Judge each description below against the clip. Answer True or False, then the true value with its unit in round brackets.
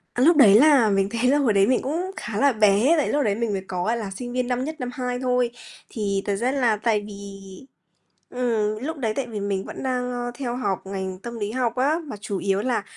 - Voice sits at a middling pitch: False (235 Hz)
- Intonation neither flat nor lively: True (4.0 semitones)